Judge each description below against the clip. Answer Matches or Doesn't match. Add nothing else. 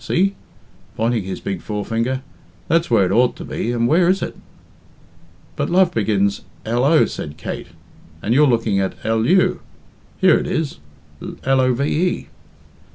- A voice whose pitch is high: Doesn't match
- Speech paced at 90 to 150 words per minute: Matches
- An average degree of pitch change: Doesn't match